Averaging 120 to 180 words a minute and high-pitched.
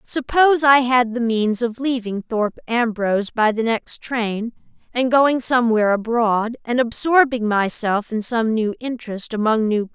Yes: average, 165 wpm; high, 235 Hz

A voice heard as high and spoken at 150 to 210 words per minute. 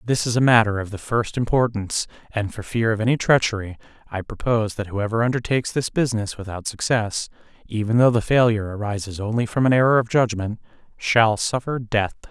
No: low, 110 Hz; average, 180 wpm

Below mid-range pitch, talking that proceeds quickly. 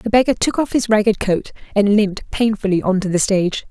No: high, 205 Hz; fast, 225 wpm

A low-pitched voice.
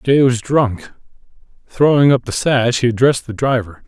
Yes: low, 125 Hz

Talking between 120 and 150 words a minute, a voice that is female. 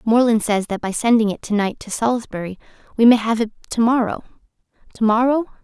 No: average, 160 wpm; female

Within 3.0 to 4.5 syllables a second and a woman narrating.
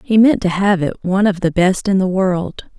No: 4.9 syllables/s; female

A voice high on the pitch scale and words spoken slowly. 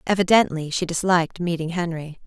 No: medium, 170 Hz; slow, 130 wpm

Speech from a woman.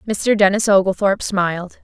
Yes: female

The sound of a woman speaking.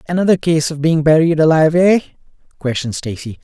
No: male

